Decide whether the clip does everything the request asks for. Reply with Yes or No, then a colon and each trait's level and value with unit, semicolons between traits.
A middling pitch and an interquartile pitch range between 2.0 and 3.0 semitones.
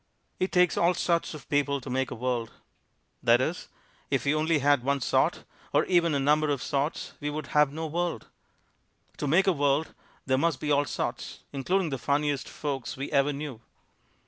Yes: medium, 145 Hz; narrow, 2.6 semitones